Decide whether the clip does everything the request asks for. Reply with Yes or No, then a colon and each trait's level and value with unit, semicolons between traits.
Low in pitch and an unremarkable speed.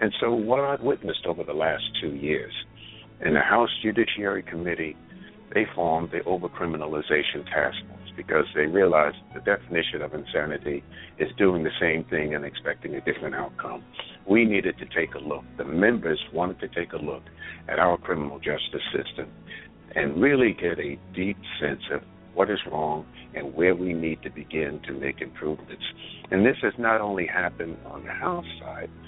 Yes: very low, 85 Hz; average, 175 wpm